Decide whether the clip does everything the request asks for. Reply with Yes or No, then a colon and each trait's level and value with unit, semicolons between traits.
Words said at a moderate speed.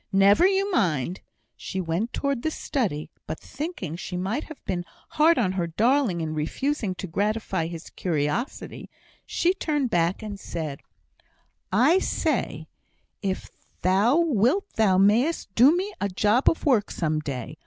Yes: average, 150 wpm